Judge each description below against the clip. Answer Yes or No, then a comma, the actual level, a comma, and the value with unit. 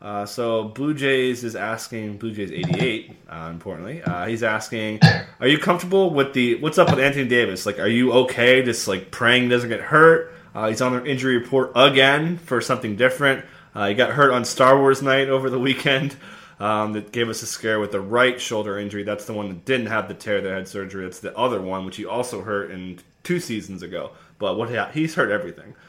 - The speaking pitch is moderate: No, low, 120 Hz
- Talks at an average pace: No, fast, 220 wpm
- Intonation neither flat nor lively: Yes, average, 4.4 semitones